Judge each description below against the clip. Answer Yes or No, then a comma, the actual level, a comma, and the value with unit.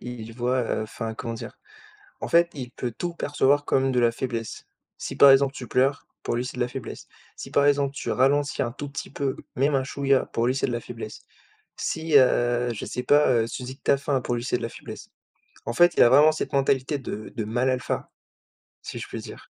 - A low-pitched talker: Yes, low, 130 Hz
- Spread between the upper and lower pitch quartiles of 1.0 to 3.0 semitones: Yes, narrow, 2.6 semitones